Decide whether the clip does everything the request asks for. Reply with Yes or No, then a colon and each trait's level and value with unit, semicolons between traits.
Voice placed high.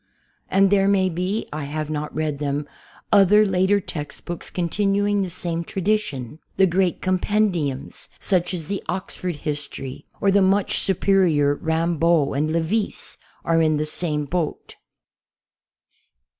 No: medium, 175 Hz